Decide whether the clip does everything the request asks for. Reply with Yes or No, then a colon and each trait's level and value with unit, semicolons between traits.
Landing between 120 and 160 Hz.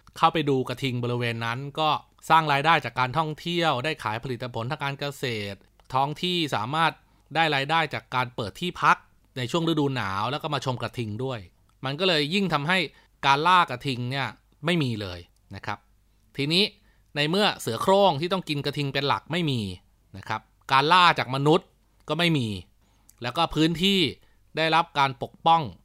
Yes: medium, 140 Hz